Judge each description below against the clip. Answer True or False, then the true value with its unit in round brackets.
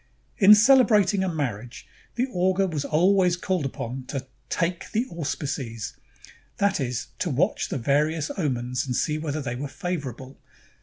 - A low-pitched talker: False (155 Hz)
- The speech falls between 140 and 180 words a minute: True (150 wpm)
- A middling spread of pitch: False (6.0 semitones)